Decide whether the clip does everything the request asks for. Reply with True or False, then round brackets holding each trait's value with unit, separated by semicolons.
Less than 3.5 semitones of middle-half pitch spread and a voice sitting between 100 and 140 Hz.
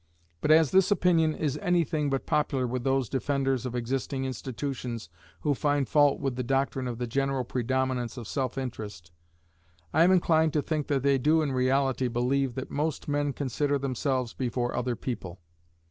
True (2.5 semitones; 135 Hz)